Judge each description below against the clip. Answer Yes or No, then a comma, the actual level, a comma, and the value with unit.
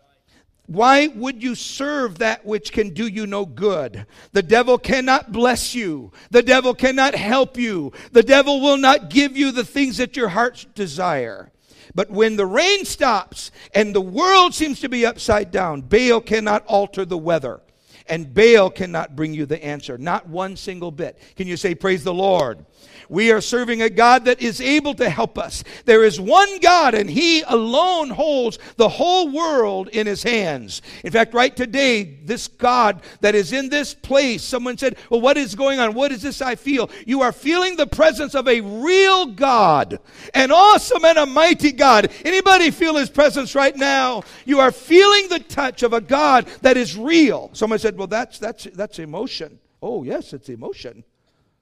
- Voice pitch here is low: No, high, 245 Hz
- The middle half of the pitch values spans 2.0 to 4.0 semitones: No, average, 5.2 semitones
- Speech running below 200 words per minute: Yes, average, 185 wpm